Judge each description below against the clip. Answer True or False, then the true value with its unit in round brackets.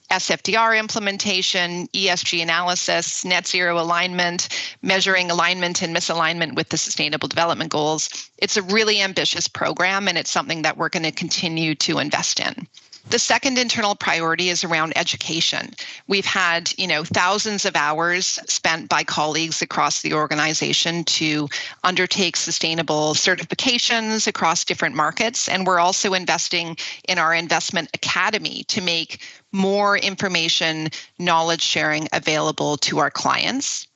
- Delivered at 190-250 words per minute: False (135 wpm)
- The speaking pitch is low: False (175 Hz)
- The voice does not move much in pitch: False (3.0 semitones)